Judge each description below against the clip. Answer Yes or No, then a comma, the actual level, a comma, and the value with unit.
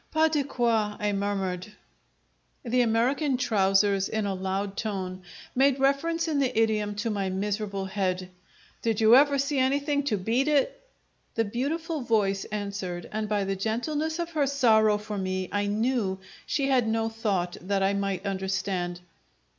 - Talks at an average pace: Yes, average, 160 wpm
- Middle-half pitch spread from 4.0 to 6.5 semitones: Yes, average, 5.2 semitones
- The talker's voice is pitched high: Yes, high, 215 Hz